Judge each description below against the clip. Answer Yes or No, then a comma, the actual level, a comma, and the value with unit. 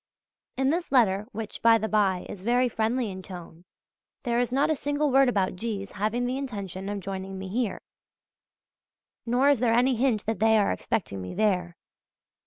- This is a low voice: No, high, 220 Hz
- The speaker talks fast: No, average, 185 wpm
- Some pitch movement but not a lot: Yes, average, 4.3 semitones